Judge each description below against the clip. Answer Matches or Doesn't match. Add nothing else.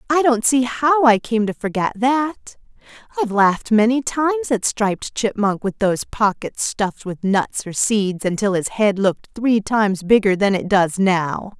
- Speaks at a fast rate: Doesn't match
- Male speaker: Doesn't match